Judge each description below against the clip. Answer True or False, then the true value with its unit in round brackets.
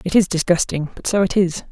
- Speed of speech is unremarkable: False (245 wpm)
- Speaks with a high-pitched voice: False (180 Hz)